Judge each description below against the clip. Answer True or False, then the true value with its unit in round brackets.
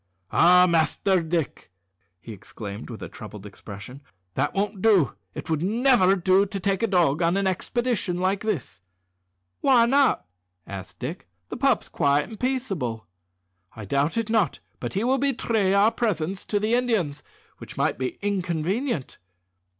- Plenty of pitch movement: True (7.2 semitones)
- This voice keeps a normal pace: True (155 wpm)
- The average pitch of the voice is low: False (185 Hz)